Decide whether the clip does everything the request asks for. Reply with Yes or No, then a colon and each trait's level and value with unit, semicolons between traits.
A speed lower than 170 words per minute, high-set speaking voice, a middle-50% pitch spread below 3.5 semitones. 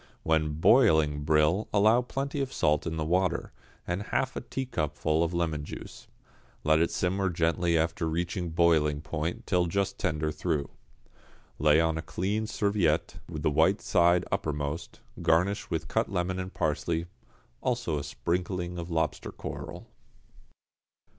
No: average, 140 wpm; very low, 85 Hz; average, 3.1 semitones